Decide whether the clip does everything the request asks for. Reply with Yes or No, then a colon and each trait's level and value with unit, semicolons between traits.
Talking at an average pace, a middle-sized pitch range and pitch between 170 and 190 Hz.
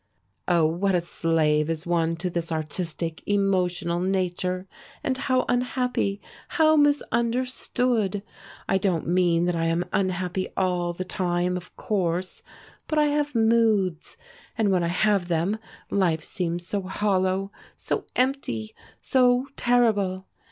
No: slow, 130 wpm; average, 4.3 semitones; medium, 185 Hz